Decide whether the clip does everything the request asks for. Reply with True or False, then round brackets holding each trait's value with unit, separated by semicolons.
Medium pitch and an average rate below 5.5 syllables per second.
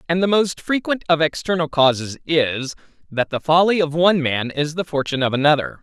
False (160 Hz; 5.6 syllables/s)